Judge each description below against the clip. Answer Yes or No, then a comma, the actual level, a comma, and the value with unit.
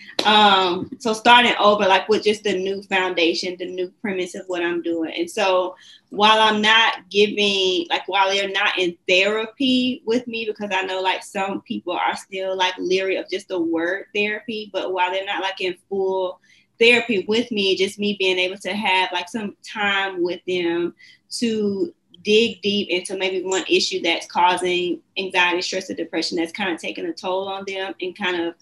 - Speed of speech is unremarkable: Yes, average, 190 wpm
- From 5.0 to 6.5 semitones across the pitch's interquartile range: No, narrow, 2.5 semitones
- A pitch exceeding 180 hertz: Yes, high, 190 Hz